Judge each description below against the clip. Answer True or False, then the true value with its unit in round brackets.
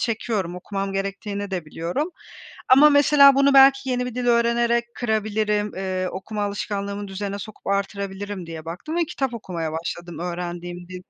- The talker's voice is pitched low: False (205 Hz)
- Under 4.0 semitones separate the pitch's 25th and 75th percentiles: False (4.3 semitones)